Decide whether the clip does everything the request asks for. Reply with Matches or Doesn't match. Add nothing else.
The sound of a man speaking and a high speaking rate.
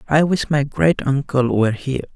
Doesn't match